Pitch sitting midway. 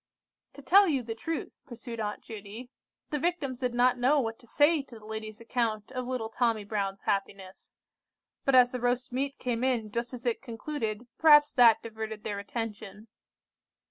No: high, 235 Hz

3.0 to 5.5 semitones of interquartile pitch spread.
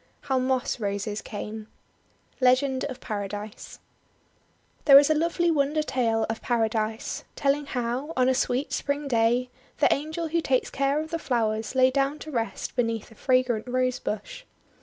Yes: average, 3.9 semitones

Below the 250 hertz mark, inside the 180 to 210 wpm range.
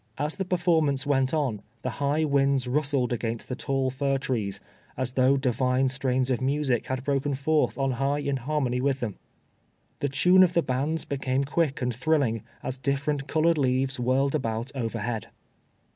No: low, 135 Hz; average, 170 wpm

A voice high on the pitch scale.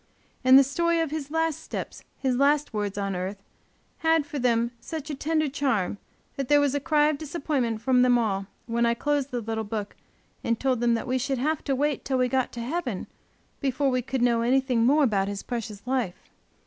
Yes: very high, 260 Hz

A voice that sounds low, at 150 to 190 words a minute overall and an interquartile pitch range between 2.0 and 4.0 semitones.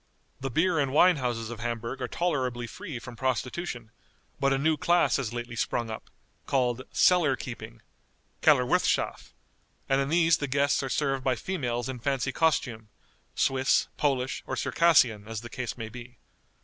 Yes: low, 130 Hz; average, 160 wpm; average, 3.4 semitones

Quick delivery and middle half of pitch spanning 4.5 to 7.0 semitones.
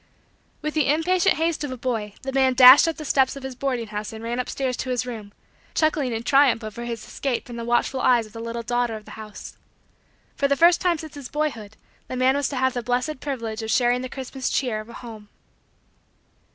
No: fast, 230 wpm; average, 3.2 semitones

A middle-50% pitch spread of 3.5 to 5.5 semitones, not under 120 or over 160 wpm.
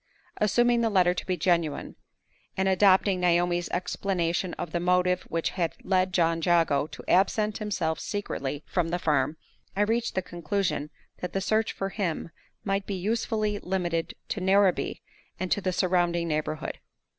No: average, 2.7 semitones; average, 155 wpm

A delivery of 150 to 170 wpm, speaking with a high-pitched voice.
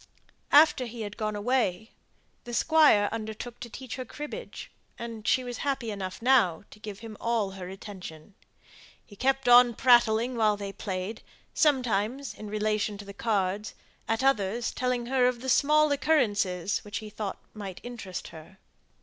Yes: average, 160 wpm; high, 220 Hz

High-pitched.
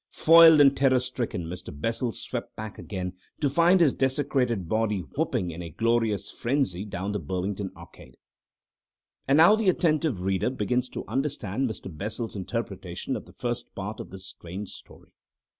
No: low, 110 Hz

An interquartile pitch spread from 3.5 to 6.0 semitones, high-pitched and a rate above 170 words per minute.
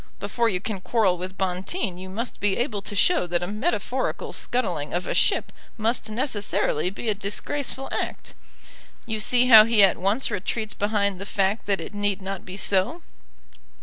No: average, 3.1 semitones; high, 205 Hz; average, 180 wpm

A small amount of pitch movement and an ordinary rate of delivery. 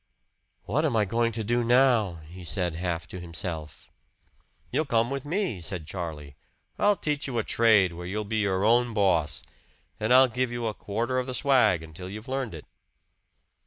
No: wide, 5.6 semitones; average, 185 wpm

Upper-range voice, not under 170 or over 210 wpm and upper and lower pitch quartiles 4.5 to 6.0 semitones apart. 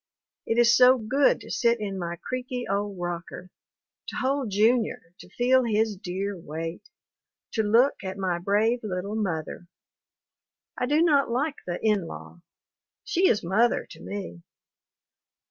No: high, 215 Hz; average, 145 wpm; average, 5.1 semitones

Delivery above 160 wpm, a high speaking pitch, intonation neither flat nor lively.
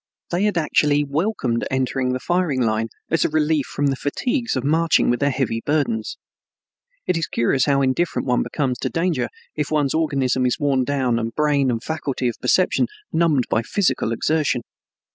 No: average, 180 wpm; medium, 140 Hz; average, 3.7 semitones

